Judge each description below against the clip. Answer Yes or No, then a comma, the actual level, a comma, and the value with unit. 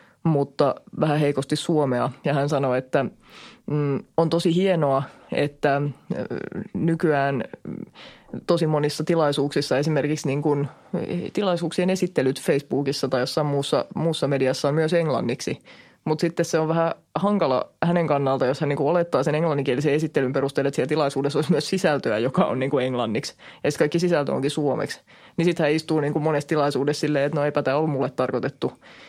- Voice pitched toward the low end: No, medium, 150 Hz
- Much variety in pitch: No, average, 2.9 semitones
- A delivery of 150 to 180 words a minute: Yes, fast, 155 wpm